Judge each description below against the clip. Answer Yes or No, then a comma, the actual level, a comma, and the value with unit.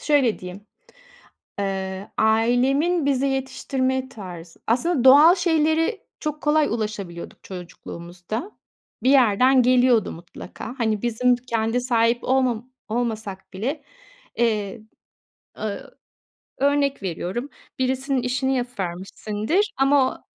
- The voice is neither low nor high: No, high, 245 Hz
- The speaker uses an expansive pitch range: No, average, 4.3 semitones